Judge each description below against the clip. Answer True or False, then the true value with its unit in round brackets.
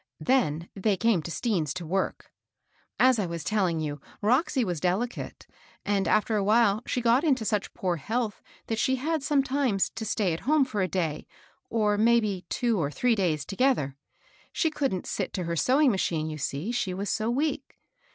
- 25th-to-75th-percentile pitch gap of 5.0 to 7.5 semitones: True (5.5 semitones)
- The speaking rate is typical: True (195 wpm)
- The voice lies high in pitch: True (210 Hz)